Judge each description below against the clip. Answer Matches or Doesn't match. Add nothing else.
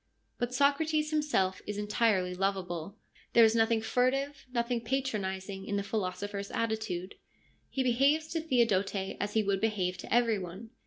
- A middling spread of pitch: Matches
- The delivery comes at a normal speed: Matches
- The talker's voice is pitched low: Doesn't match